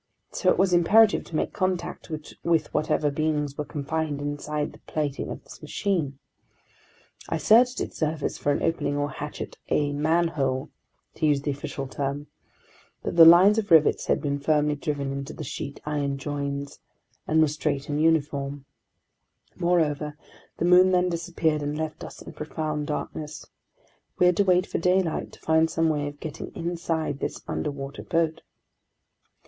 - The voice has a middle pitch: Yes, medium, 155 Hz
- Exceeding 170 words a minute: No, average, 165 wpm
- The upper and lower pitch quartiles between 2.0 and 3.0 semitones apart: Yes, narrow, 2.6 semitones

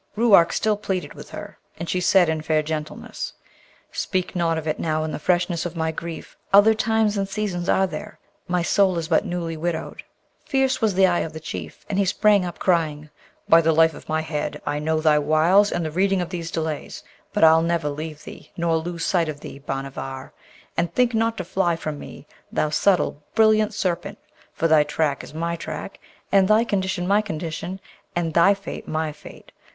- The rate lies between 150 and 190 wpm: No, average, 200 wpm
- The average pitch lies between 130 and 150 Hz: No, medium, 170 Hz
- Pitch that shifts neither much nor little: Yes, average, 3.5 semitones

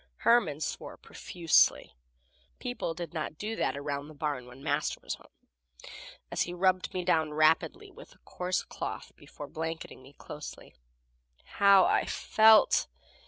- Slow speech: No, average, 145 wpm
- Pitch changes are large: No, average, 4.2 semitones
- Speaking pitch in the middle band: Yes, medium, 160 Hz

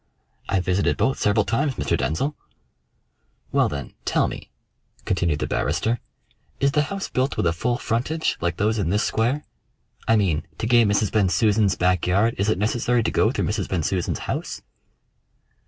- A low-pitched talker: Yes, low, 105 Hz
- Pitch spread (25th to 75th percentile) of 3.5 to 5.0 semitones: Yes, average, 4.6 semitones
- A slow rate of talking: No, average, 170 wpm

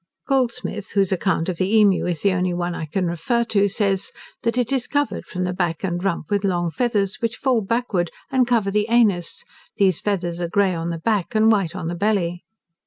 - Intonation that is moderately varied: Yes, average, 4.1 semitones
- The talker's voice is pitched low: No, high, 195 Hz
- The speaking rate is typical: No, fast, 215 wpm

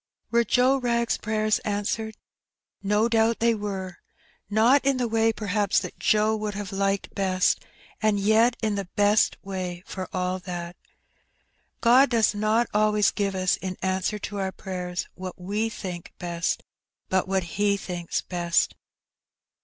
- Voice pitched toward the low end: No, high, 205 Hz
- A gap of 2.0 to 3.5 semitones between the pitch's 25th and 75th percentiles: Yes, average, 2.8 semitones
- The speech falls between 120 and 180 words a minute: Yes, average, 150 wpm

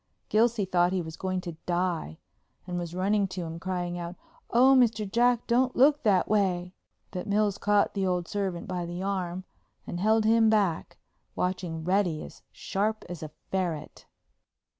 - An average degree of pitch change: Yes, average, 3.3 semitones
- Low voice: No, medium, 185 Hz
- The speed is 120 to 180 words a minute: Yes, average, 170 wpm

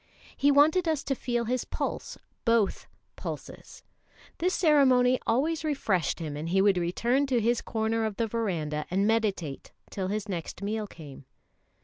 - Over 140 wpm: Yes, average, 155 wpm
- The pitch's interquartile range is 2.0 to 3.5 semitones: No, wide, 5.6 semitones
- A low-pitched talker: No, high, 225 Hz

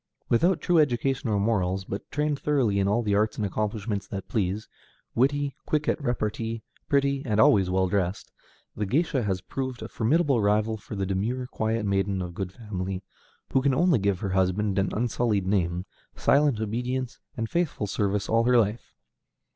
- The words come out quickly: No, average, 175 wpm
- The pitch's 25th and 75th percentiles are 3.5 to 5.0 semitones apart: Yes, average, 4.6 semitones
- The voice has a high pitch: No, low, 110 Hz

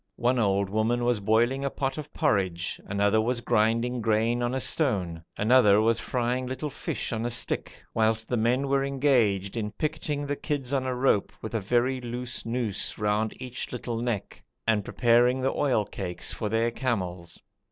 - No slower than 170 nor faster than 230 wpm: Yes, average, 180 wpm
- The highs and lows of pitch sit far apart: No, average, 3.1 semitones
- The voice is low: Yes, low, 120 Hz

